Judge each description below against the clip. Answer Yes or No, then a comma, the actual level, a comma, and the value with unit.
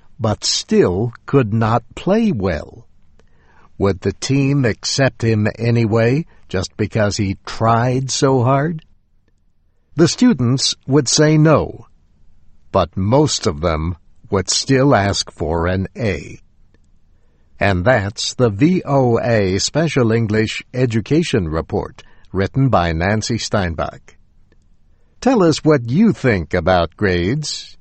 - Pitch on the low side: Yes, low, 110 Hz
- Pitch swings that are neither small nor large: No, wide, 6.7 semitones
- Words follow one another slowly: Yes, slow, 110 wpm